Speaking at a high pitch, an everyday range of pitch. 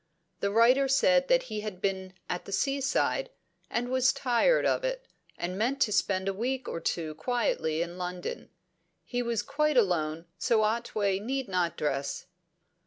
No: high, 220 Hz; wide, 6.1 semitones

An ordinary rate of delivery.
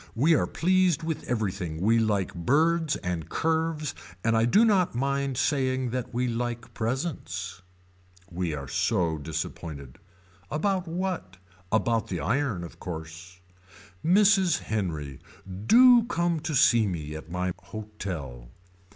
No: slow, 130 wpm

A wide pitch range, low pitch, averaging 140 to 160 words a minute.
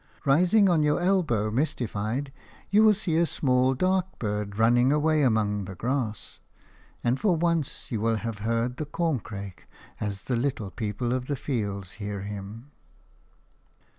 Yes: wide, 6.5 semitones; low, 125 Hz; average, 150 wpm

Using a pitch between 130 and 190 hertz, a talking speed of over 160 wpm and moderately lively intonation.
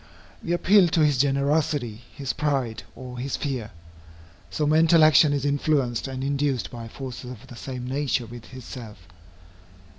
No: low, 135 Hz; average, 150 wpm; average, 3.1 semitones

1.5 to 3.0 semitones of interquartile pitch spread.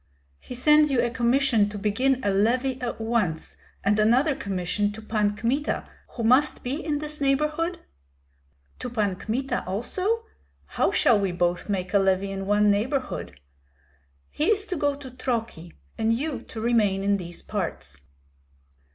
No: average, 5.1 semitones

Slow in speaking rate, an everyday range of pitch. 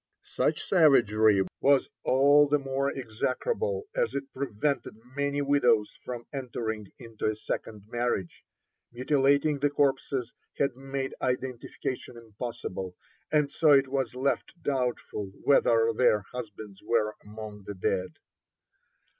Yes: slow, 120 wpm; average, 4.4 semitones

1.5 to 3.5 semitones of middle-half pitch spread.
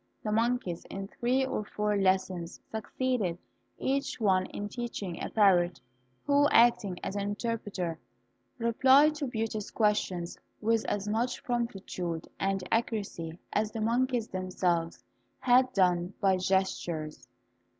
No: average, 4.2 semitones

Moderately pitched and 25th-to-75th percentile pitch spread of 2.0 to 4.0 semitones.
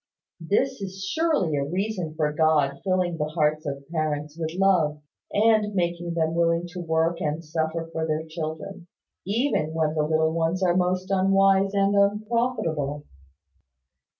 Yes: medium, 170 Hz; average, 3.7 semitones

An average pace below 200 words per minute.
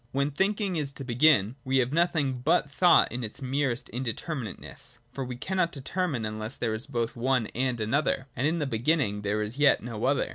No: fast, 205 wpm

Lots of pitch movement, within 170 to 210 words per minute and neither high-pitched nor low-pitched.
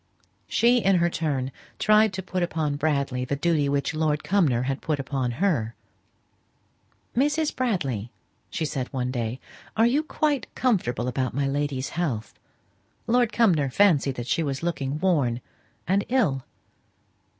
No: wide, 6.6 semitones; average, 145 wpm; medium, 150 Hz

